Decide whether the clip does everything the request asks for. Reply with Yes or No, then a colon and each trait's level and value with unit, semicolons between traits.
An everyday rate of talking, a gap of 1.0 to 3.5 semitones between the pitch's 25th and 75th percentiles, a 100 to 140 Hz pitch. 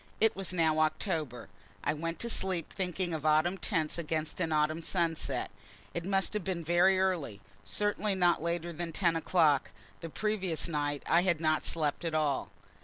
No: average, 175 wpm; average, 3.0 semitones; medium, 170 Hz